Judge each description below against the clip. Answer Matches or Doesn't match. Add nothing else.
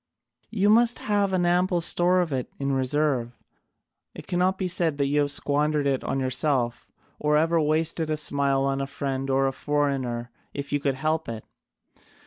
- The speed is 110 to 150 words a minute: Doesn't match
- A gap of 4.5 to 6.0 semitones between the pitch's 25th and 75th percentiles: Doesn't match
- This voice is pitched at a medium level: Matches